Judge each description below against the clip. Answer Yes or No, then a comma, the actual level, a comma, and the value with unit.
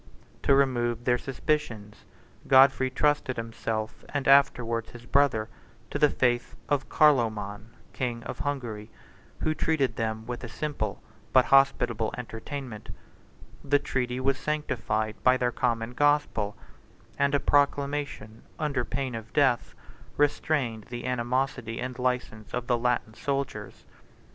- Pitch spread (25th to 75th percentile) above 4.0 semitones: No, average, 3.5 semitones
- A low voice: Yes, low, 125 Hz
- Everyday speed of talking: No, slow, 130 wpm